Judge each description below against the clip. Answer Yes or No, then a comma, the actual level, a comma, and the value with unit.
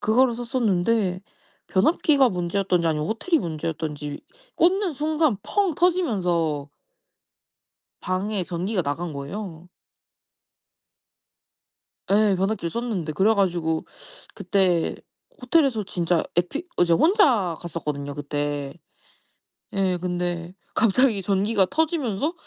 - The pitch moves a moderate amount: No, wide, 5.9 semitones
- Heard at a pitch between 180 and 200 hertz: Yes, high, 190 Hz